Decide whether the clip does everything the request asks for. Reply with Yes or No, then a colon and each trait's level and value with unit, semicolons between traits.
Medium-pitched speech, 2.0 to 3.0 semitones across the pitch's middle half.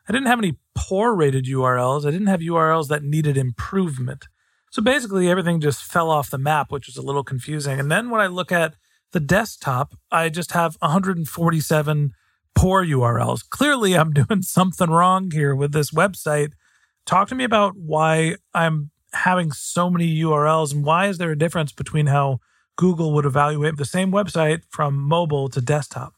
No: medium, 160 Hz; average, 3.9 semitones